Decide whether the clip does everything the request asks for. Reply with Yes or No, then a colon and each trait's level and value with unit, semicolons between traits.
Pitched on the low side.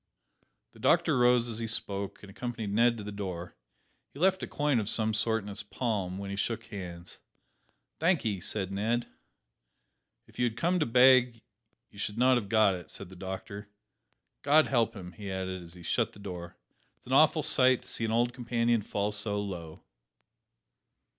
Yes: low, 110 Hz